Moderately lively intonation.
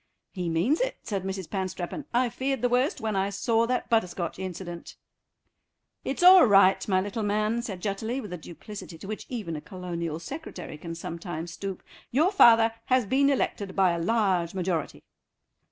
Yes: average, 5.0 semitones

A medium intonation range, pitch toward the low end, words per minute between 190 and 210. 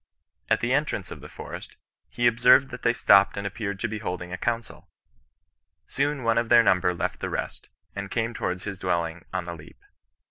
Yes: average, 4.5 semitones; low, 105 Hz; average, 200 wpm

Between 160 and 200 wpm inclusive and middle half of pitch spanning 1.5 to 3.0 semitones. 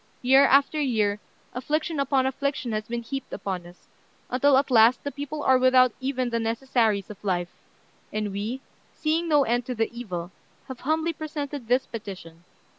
No: average, 170 wpm; average, 4.4 semitones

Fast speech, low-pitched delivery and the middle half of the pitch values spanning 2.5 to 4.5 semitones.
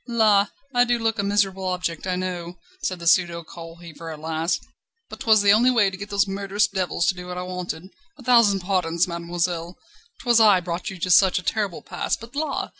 No: fast, 215 wpm; medium, 185 Hz; average, 3.0 semitones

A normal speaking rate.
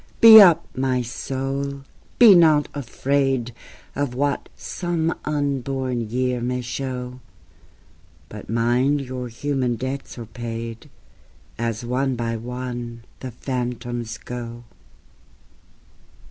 No: slow, 105 wpm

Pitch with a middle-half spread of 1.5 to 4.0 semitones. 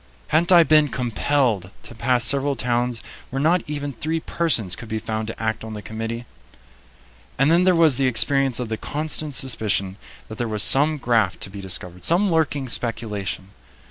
No: average, 5.0 semitones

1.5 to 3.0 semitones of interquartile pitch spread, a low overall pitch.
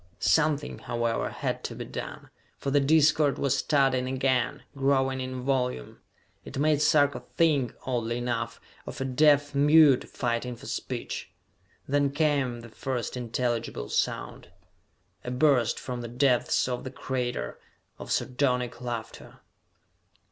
Yes: narrow, 2.5 semitones; low, 130 Hz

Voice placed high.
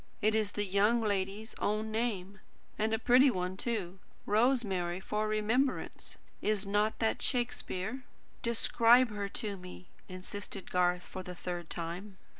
Yes: high, 205 Hz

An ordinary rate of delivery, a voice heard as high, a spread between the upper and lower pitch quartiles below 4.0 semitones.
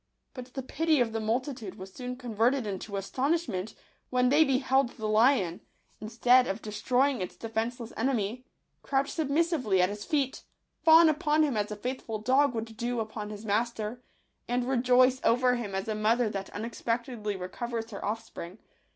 Yes: average, 170 wpm; high, 235 Hz; average, 3.5 semitones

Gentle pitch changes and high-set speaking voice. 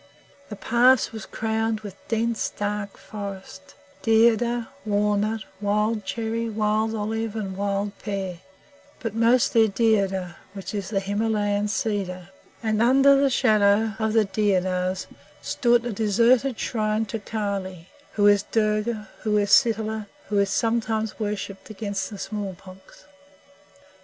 Yes: narrow, 1.9 semitones; high, 215 Hz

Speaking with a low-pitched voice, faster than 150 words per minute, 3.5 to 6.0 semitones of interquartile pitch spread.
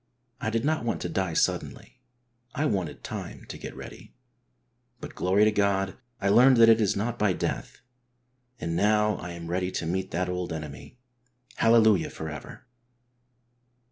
Yes: low, 100 Hz; average, 165 wpm; average, 3.9 semitones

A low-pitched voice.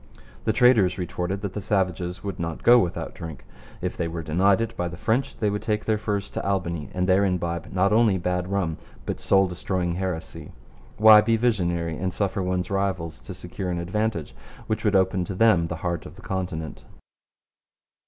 Yes: very low, 95 Hz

